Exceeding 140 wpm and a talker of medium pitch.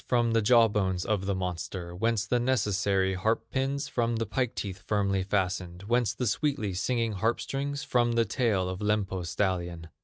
No: average, 180 wpm; low, 105 Hz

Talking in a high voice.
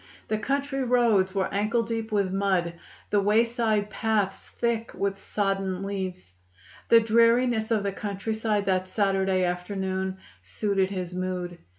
Yes: high, 200 Hz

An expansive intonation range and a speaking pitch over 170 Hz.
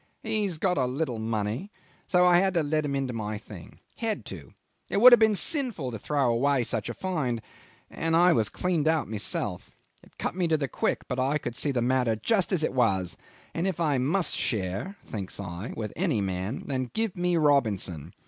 No: wide, 7.8 semitones; medium, 140 Hz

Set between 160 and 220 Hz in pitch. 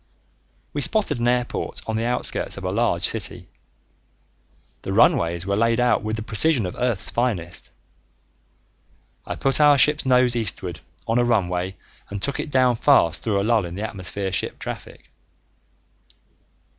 No: low, 115 Hz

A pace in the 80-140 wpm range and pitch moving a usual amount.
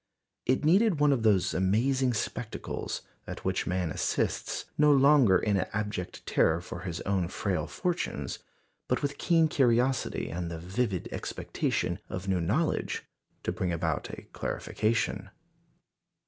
No: slow, 135 wpm; wide, 7.1 semitones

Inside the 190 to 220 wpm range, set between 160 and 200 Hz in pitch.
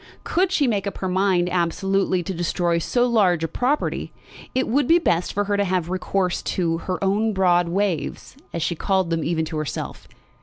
Yes: average, 195 wpm; medium, 185 Hz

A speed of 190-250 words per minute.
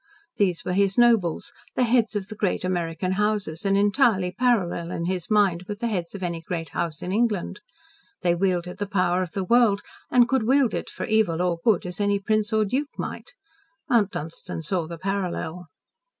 Yes: average, 195 wpm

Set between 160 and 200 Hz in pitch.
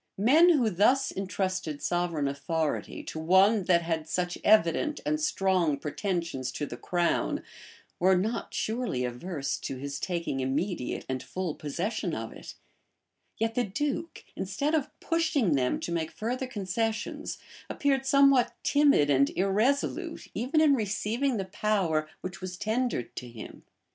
Yes: high, 190 Hz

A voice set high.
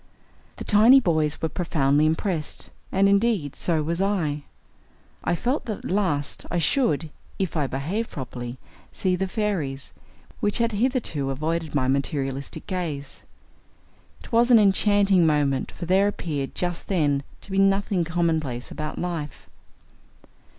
No: medium, 170 Hz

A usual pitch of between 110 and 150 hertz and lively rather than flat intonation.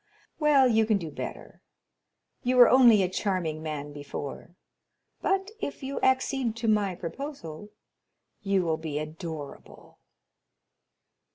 No: high, 195 Hz; wide, 8.2 semitones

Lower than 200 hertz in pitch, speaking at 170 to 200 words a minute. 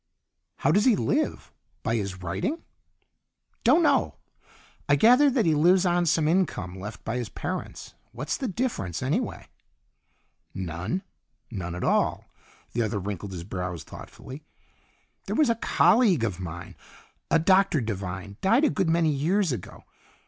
No: medium, 140 Hz; average, 150 wpm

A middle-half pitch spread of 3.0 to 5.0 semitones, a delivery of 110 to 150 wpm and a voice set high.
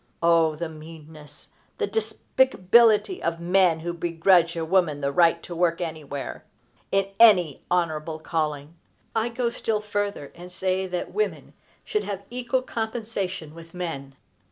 No: average, 4.2 semitones; average, 140 wpm; medium, 175 Hz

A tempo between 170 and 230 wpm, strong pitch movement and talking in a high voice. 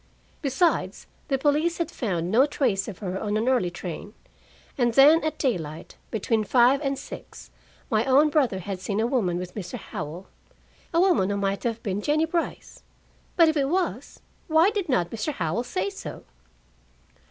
Yes: average, 175 wpm; wide, 7.4 semitones; high, 235 Hz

